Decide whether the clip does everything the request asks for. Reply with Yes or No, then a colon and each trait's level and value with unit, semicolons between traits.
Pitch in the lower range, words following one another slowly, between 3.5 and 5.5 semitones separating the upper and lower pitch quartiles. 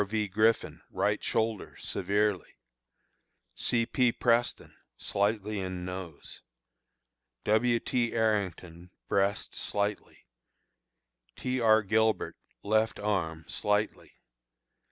No: low, 105 Hz; slow, 90 wpm; narrow, 2.5 semitones